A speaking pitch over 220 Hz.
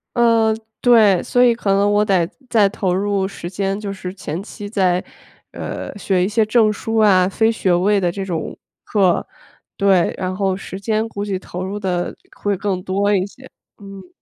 No: high, 200 Hz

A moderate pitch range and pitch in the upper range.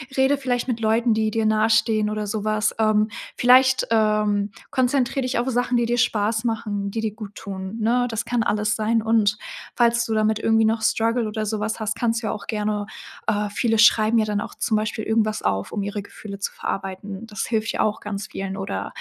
No: narrow, 1.6 semitones; high, 220 Hz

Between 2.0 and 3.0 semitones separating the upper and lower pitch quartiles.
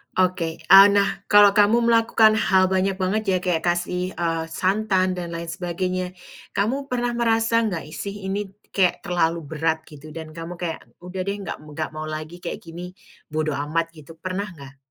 No: average, 3.4 semitones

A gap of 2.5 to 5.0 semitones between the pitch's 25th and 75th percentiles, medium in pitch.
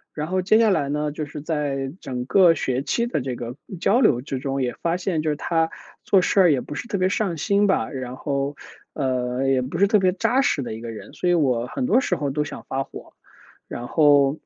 No: wide, 5.5 semitones; medium, 150 Hz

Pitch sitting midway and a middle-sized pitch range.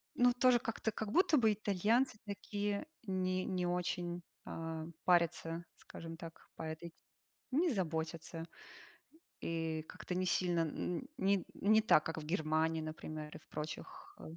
Yes: medium, 175 Hz; average, 4.0 semitones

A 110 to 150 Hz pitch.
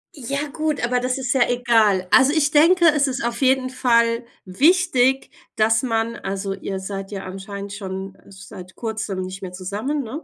No: high, 235 Hz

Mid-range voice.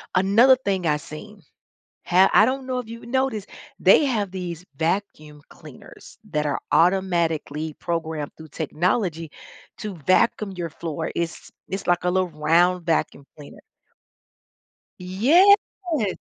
Yes: medium, 180 Hz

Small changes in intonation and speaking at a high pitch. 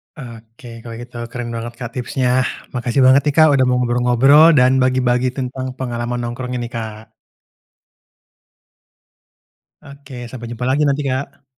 No: narrow, 1.7 semitones; low, 125 Hz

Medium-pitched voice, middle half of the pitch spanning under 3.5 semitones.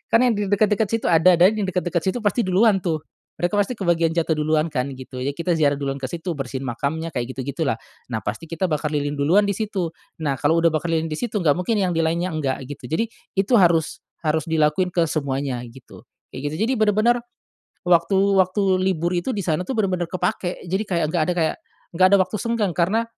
No: medium, 170 Hz; average, 4.2 semitones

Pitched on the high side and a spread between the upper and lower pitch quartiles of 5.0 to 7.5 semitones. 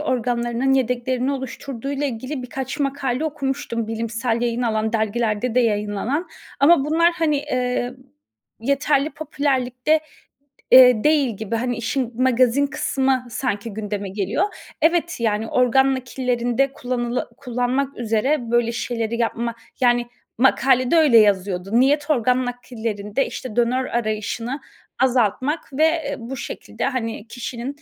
No: very high, 250 Hz; average, 2.8 semitones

